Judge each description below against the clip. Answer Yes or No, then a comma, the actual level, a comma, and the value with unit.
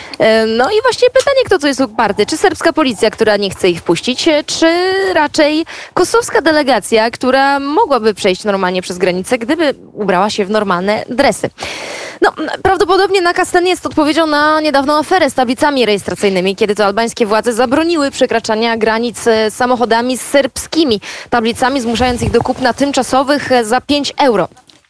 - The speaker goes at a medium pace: Yes, average, 150 wpm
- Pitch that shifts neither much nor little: No, wide, 5.9 semitones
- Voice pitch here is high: Yes, very high, 255 Hz